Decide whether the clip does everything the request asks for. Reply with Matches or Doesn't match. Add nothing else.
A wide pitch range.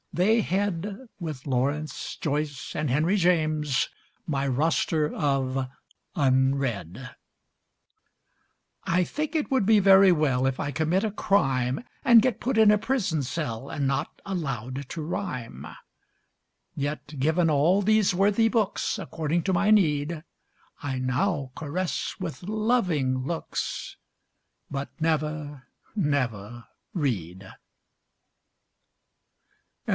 Matches